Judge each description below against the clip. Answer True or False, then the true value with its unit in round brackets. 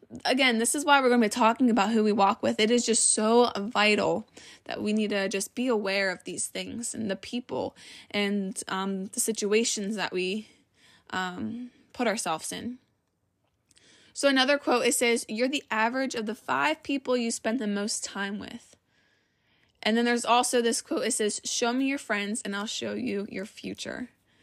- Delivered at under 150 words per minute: False (190 wpm)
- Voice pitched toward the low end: False (225 Hz)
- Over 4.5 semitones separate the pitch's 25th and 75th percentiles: False (3.0 semitones)